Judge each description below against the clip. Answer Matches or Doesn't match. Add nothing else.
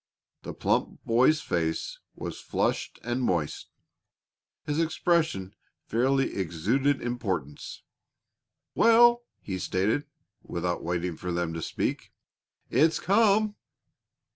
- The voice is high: Doesn't match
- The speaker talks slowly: Matches